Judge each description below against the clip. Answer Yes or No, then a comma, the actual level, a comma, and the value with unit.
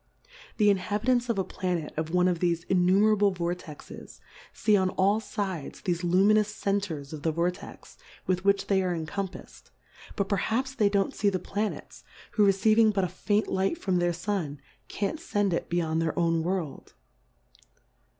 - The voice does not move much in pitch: No, average, 3.0 semitones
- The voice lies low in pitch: No, high, 190 Hz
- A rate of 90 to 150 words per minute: No, average, 160 wpm